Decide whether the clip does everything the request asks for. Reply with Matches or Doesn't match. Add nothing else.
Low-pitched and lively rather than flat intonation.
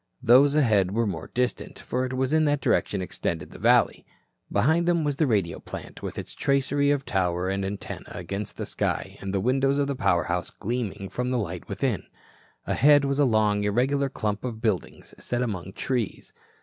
Matches